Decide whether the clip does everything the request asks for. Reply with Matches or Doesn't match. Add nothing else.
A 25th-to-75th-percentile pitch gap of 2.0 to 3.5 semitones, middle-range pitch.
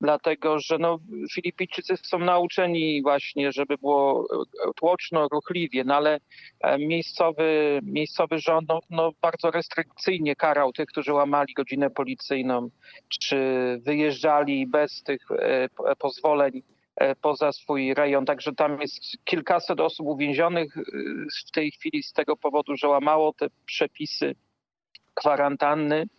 Matches